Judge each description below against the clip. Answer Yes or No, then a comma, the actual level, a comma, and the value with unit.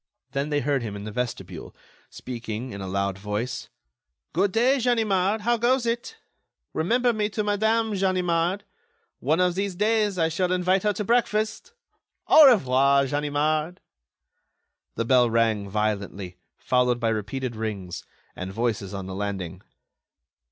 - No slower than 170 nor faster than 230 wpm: No, average, 145 wpm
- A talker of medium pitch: Yes, medium, 145 Hz